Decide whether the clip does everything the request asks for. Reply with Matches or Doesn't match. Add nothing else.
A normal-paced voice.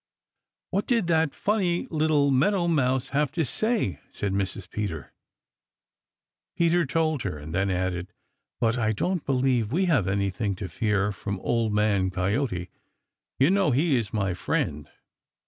Matches